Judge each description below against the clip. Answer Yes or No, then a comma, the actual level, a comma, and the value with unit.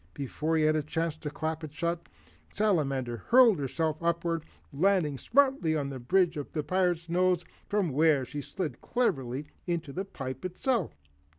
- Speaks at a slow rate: No, average, 170 wpm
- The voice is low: No, medium, 160 Hz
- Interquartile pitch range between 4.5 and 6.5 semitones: No, average, 4.1 semitones